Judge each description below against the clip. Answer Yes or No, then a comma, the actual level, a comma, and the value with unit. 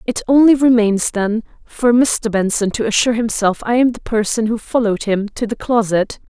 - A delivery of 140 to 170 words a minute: No, average, 190 wpm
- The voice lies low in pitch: No, high, 225 Hz